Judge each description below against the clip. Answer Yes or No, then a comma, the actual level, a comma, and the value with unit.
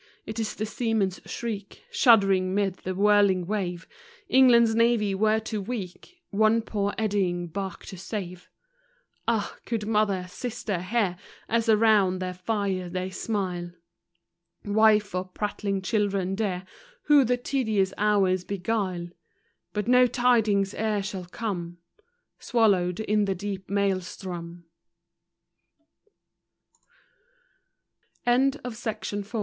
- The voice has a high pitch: Yes, high, 205 Hz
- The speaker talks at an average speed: No, slow, 110 wpm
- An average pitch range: Yes, average, 3.0 semitones